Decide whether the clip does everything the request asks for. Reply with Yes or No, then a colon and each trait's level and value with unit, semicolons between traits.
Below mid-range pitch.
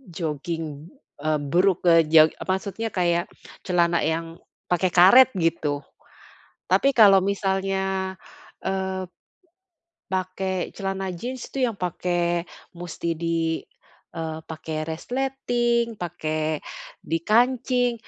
No: medium, 185 Hz